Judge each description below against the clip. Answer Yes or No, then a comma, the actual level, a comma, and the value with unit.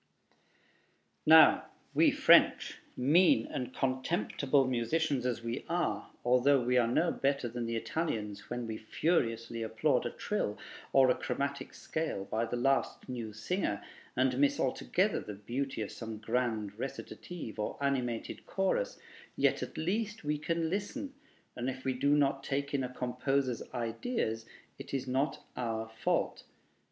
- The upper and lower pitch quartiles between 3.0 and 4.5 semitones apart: Yes, average, 3.6 semitones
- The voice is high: No, low, 130 Hz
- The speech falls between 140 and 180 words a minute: Yes, average, 145 wpm